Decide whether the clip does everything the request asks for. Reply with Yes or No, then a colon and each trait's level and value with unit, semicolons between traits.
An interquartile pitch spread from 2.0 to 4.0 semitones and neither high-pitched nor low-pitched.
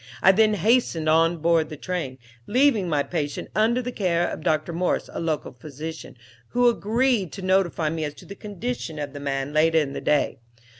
No: average, 5.1 semitones; medium, 170 Hz